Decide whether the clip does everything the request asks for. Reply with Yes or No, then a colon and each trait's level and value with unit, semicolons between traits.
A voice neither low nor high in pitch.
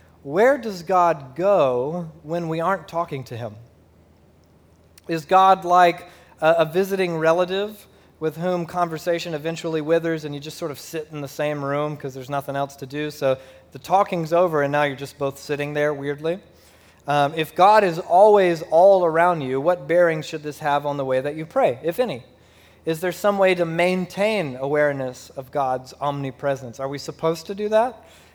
Yes: medium, 160 Hz